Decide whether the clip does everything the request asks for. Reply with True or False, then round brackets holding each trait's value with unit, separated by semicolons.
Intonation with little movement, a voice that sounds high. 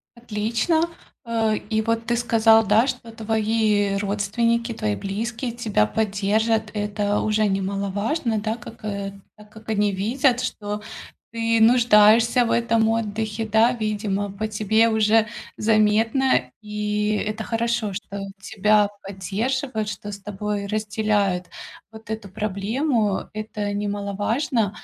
True (1.8 semitones; 215 Hz)